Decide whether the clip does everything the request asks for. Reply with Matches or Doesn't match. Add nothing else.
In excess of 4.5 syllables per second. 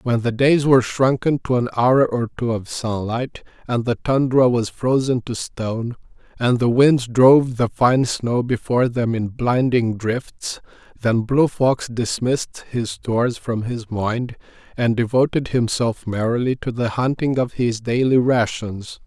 Doesn't match